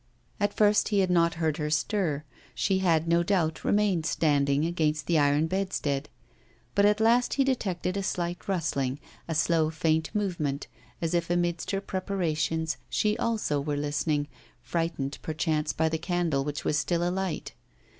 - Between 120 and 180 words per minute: Yes, average, 160 wpm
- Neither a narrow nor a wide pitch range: Yes, average, 3.7 semitones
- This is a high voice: No, medium, 165 Hz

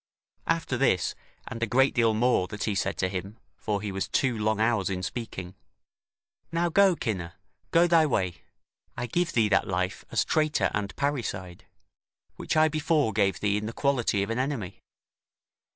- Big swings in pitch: Yes, wide, 6.1 semitones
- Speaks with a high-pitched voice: No, low, 110 Hz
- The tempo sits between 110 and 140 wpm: No, average, 175 wpm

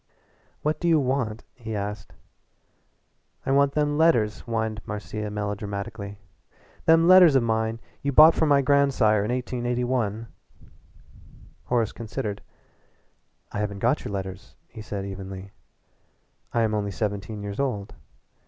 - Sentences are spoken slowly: Yes, slow, 130 wpm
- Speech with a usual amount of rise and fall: Yes, average, 4.9 semitones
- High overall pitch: No, low, 110 Hz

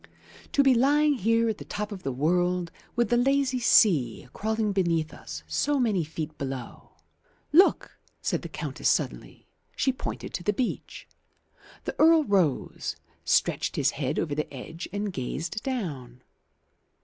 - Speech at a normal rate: Yes, average, 155 wpm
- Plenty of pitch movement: Yes, wide, 8.2 semitones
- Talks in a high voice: Yes, high, 200 Hz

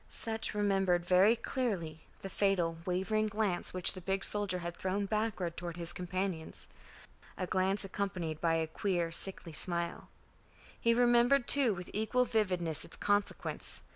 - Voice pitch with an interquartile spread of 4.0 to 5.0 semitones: No, average, 3.3 semitones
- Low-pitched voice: No, high, 190 Hz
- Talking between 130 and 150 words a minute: Yes, average, 145 wpm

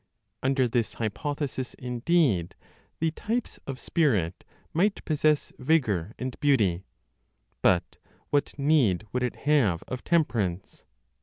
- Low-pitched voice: Yes, low, 130 Hz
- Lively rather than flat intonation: Yes, wide, 6.4 semitones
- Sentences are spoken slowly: Yes, slow, 110 wpm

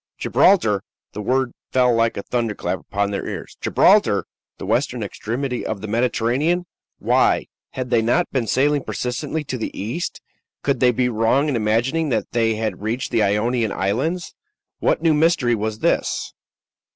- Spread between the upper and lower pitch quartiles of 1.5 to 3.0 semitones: No, average, 3.8 semitones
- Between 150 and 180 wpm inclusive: Yes, average, 160 wpm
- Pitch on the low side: Yes, low, 120 Hz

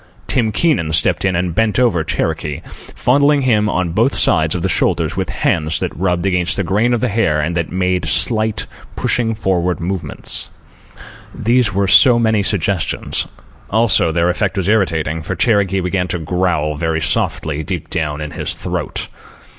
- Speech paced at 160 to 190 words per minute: Yes, average, 170 wpm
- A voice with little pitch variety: No, average, 4.9 semitones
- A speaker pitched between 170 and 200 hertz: No, very low, 95 Hz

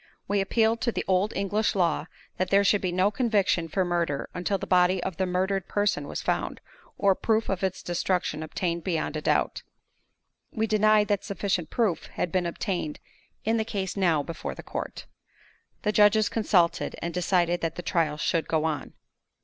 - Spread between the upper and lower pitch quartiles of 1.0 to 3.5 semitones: Yes, average, 3.1 semitones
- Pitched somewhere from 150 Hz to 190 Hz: Yes, medium, 185 Hz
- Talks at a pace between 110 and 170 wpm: No, average, 180 wpm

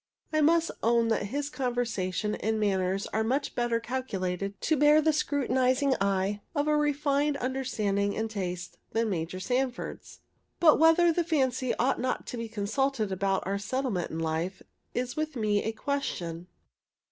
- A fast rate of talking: No, average, 160 wpm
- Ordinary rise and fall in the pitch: No, wide, 5.9 semitones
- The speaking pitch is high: Yes, high, 235 Hz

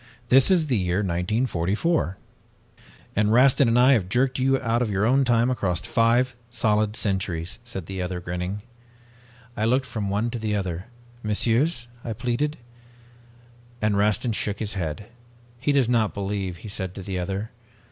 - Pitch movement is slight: No, average, 4.2 semitones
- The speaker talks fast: No, average, 165 wpm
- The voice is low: Yes, low, 110 Hz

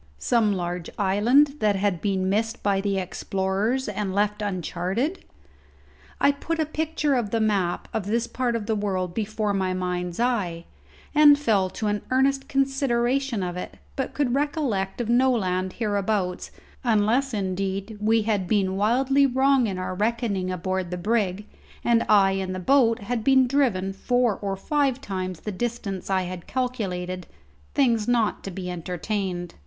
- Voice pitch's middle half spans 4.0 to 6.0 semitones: Yes, average, 4.6 semitones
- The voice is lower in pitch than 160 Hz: No, high, 210 Hz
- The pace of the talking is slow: No, average, 160 wpm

